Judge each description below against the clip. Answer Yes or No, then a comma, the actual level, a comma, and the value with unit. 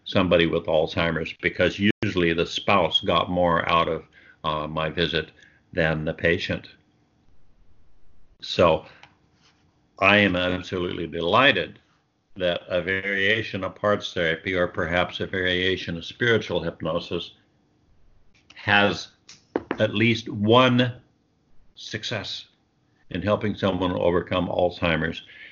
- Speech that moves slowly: Yes, slow, 105 wpm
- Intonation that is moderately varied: Yes, average, 3.5 semitones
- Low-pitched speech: Yes, very low, 90 Hz